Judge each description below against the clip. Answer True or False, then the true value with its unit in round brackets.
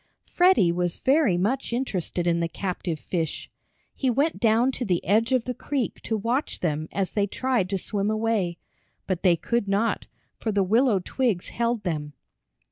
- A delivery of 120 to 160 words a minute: False (175 wpm)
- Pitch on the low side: False (210 Hz)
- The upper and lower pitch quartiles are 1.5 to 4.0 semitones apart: False (5.3 semitones)